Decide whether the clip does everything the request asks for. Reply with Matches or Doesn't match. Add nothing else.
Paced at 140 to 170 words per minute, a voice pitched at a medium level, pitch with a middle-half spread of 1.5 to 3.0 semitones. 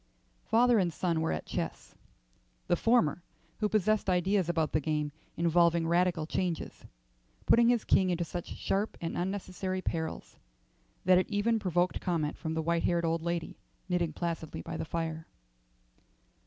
Matches